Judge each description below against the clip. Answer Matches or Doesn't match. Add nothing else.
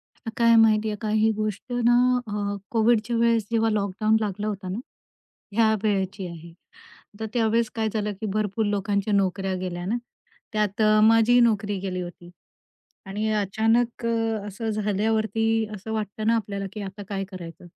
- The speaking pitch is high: Matches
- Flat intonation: Matches